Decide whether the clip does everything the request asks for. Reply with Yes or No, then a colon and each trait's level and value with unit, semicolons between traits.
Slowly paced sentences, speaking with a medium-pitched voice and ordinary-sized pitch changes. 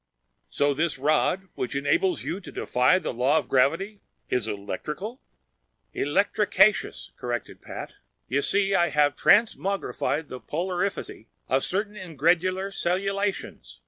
No: slow, 120 wpm; medium, 175 Hz; wide, 5.7 semitones